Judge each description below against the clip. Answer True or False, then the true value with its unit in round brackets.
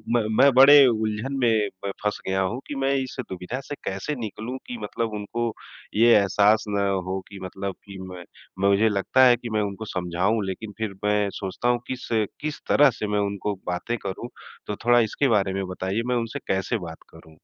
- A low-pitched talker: True (105 Hz)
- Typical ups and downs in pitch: True (3.5 semitones)